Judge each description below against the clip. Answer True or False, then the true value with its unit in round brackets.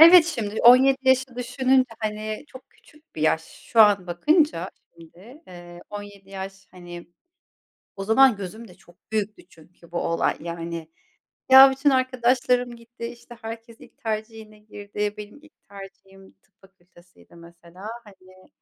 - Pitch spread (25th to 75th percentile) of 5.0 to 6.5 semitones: True (5.3 semitones)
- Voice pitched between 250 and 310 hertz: False (210 Hz)